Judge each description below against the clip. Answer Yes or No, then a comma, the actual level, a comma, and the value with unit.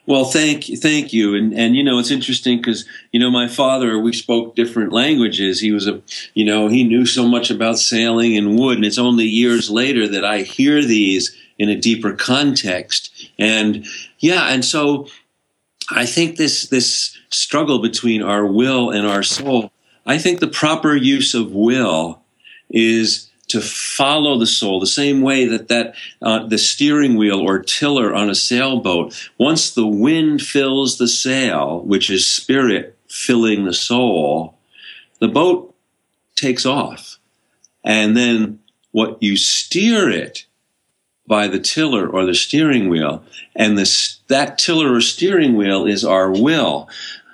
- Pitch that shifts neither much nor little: Yes, average, 3.8 semitones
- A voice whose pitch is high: No, low, 115 Hz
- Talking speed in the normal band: Yes, average, 160 wpm